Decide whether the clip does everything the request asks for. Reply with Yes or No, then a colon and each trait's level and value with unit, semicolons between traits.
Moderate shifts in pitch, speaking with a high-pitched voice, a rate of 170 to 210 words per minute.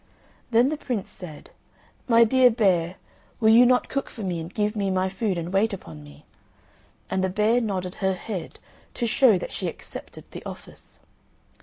Yes: average, 4.0 semitones; high, 205 Hz; average, 180 wpm